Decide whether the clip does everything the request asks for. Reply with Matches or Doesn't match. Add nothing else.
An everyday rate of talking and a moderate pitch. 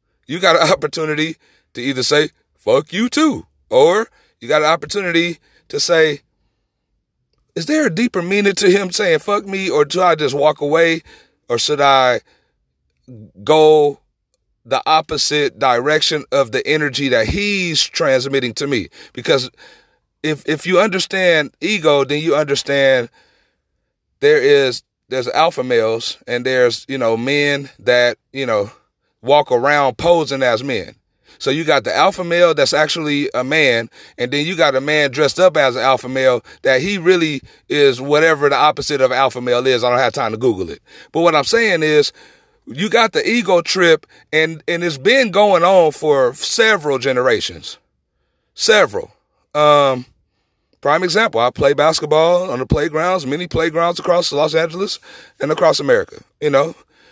Matches